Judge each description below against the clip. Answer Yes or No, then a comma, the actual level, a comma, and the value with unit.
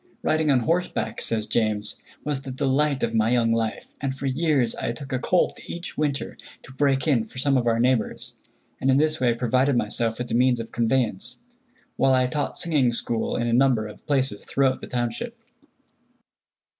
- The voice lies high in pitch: No, low, 130 Hz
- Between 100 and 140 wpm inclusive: No, average, 190 wpm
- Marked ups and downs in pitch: No, average, 3.0 semitones